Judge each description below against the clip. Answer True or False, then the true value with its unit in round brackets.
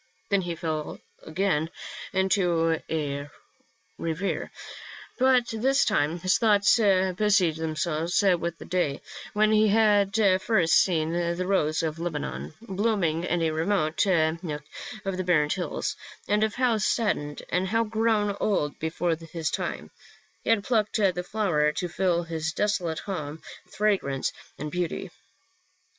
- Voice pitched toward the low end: False (180 Hz)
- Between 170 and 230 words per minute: False (135 wpm)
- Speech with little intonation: False (4.2 semitones)